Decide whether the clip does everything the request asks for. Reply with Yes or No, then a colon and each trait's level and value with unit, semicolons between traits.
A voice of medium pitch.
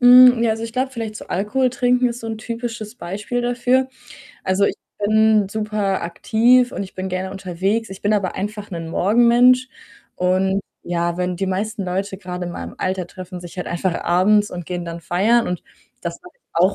No: high, 205 Hz